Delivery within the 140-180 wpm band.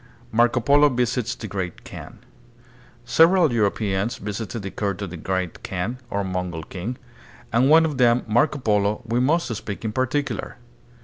Yes: average, 170 wpm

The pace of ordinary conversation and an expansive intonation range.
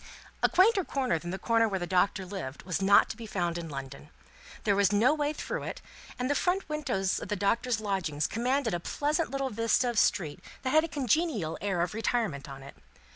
No: fast, 215 wpm; wide, 7.0 semitones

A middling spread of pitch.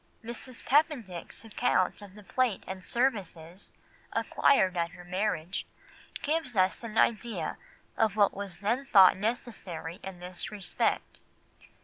Yes: average, 4.4 semitones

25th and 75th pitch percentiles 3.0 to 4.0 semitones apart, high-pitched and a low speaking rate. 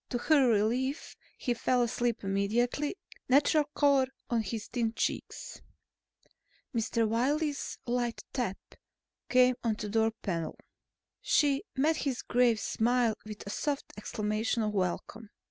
Yes: average, 3.4 semitones; high, 240 Hz; slow, 130 wpm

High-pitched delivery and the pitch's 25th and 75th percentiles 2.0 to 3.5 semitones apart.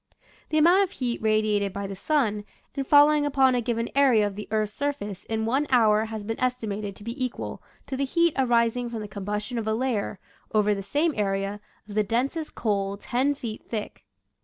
No: high, 225 Hz; average, 4.3 semitones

